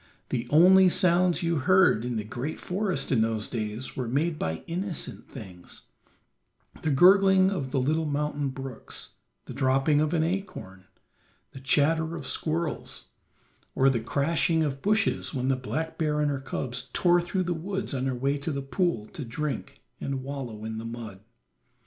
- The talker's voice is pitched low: No, medium, 145 Hz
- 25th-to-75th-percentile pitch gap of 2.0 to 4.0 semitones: No, average, 4.9 semitones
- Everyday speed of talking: Yes, average, 170 wpm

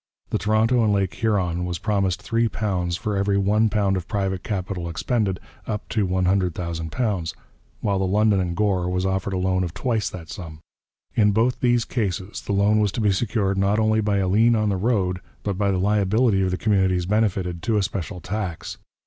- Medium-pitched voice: No, low, 100 Hz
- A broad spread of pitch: No, narrow, 2.6 semitones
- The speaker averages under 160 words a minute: No, average, 190 wpm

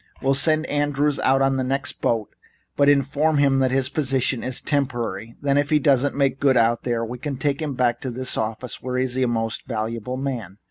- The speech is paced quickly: Yes, fast, 220 wpm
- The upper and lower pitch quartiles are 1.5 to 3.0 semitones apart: Yes, average, 2.7 semitones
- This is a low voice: Yes, low, 130 Hz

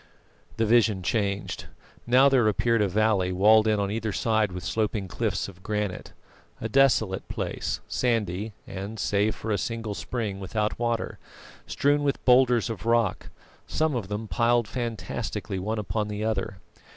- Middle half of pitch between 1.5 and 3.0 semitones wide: Yes, narrow, 2.5 semitones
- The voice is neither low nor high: No, low, 110 Hz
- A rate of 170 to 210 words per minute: No, average, 155 wpm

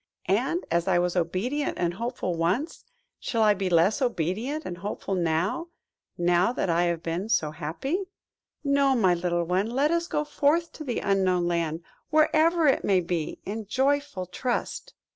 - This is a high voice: Yes, high, 195 Hz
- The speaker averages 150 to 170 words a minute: Yes, average, 160 wpm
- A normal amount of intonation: No, wide, 8.2 semitones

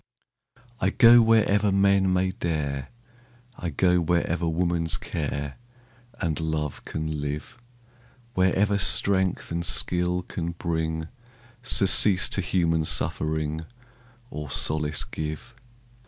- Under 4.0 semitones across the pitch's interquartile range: Yes, average, 3.4 semitones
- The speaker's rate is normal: No, slow, 105 wpm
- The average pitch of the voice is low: Yes, very low, 85 Hz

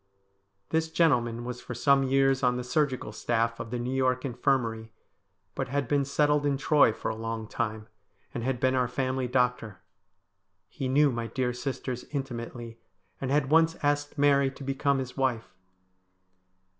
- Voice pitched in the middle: No, low, 130 Hz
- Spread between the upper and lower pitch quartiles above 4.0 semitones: No, average, 2.8 semitones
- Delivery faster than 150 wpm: Yes, average, 165 wpm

